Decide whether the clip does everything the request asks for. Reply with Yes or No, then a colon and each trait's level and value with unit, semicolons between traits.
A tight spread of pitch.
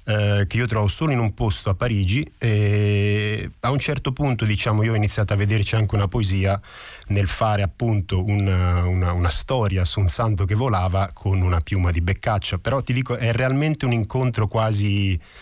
No: average, 3.0 semitones